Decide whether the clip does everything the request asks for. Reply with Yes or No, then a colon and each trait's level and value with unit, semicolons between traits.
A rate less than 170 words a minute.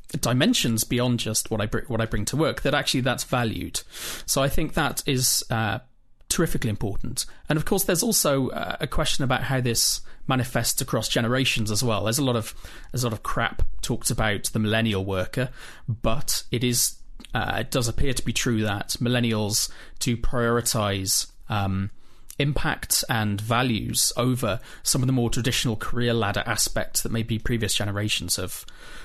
No: average, 175 wpm